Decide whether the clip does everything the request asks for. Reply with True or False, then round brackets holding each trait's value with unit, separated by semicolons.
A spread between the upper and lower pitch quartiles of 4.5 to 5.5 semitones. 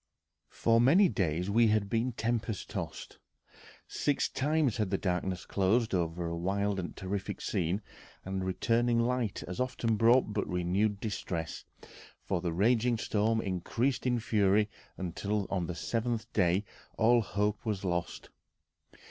False (3.9 semitones)